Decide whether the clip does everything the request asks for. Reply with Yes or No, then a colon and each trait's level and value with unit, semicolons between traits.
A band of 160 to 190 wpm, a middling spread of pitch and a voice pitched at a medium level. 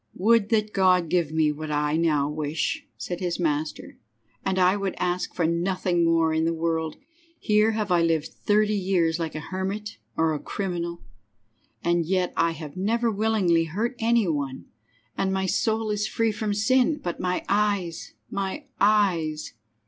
Yes: average, 170 wpm; average, 4.2 semitones; medium, 180 Hz